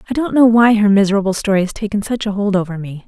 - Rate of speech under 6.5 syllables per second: No, 7.0 syllables/s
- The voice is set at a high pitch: Yes, high, 205 Hz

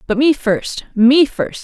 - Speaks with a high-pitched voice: Yes, very high, 255 Hz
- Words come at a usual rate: Yes, average, 145 wpm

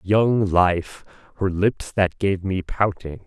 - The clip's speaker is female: No, male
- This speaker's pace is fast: No, average, 145 wpm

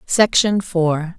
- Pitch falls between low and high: Yes, medium, 180 Hz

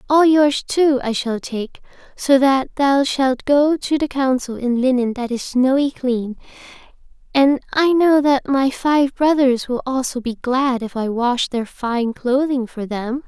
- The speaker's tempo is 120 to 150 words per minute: No, average, 175 wpm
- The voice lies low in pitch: No, very high, 260 Hz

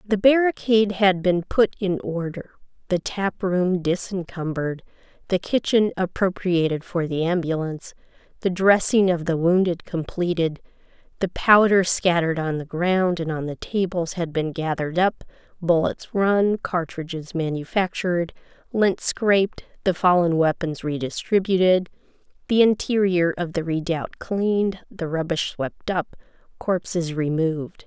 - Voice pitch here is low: No, medium, 175 Hz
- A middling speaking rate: No, slow, 130 wpm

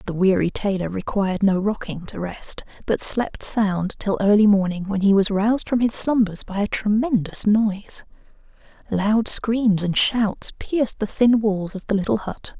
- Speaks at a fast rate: No, average, 175 wpm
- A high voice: Yes, high, 205 Hz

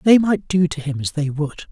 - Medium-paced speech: No, fast, 280 wpm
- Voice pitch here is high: No, medium, 160 Hz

